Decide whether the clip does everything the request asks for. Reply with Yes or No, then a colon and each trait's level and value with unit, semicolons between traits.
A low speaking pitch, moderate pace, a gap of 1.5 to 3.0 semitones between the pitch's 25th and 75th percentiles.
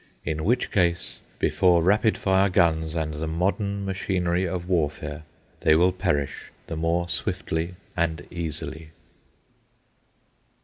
No: very low, 85 Hz; slow, 120 wpm; average, 2.7 semitones